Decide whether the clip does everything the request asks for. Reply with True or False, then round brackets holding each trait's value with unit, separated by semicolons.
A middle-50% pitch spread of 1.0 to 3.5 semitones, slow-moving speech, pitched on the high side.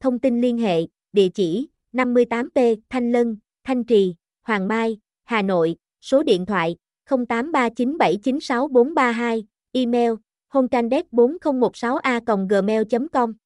True (2.9 semitones; 95 wpm; 240 Hz)